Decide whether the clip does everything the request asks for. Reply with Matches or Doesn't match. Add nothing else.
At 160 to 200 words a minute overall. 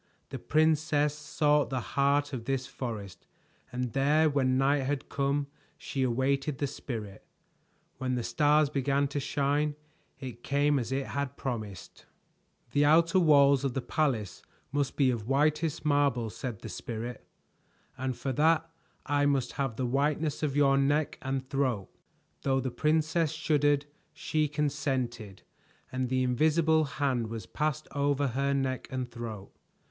Doesn't match